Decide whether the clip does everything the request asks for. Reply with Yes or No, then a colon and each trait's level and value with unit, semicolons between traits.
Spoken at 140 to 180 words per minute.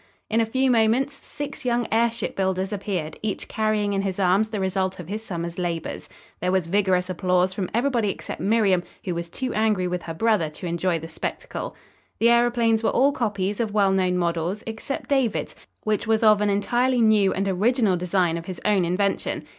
No: average, 195 wpm